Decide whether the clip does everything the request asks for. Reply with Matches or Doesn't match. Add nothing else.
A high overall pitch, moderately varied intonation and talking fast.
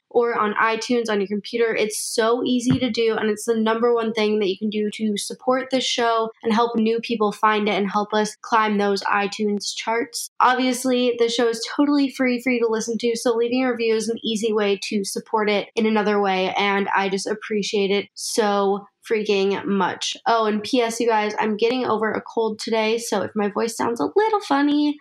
Doesn't match